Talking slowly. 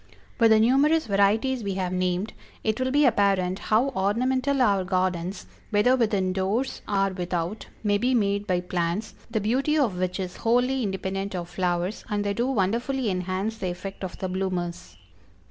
No: average, 170 wpm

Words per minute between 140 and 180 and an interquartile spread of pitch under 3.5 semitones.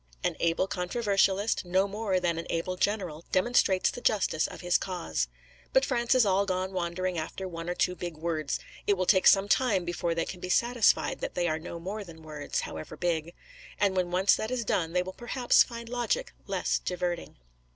No: average, 200 wpm; average, 3.1 semitones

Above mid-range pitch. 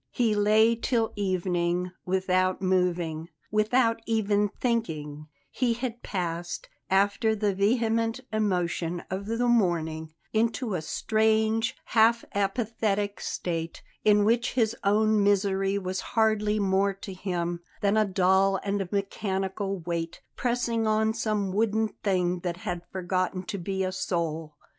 Yes: high, 200 Hz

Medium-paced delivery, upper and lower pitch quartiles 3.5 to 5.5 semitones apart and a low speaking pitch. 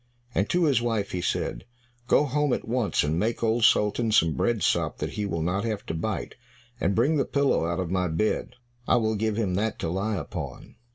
No: fast, 220 wpm; average, 4.2 semitones; low, 110 Hz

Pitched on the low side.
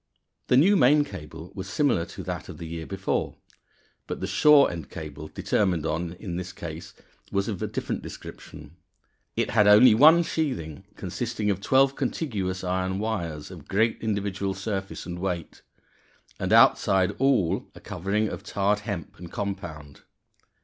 Yes: very low, 95 Hz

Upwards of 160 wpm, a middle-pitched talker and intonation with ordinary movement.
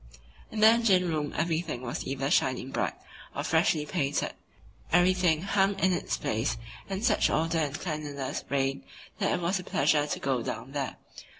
Yes: average, 170 wpm; medium, 155 Hz; average, 4.9 semitones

